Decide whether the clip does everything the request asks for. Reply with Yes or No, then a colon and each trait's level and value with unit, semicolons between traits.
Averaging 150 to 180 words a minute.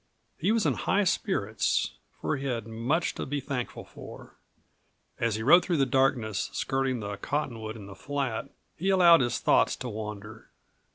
Yes: average, 170 wpm